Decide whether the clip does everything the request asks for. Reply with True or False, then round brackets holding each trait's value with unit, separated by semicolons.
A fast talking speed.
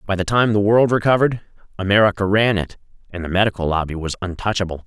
False (185 wpm)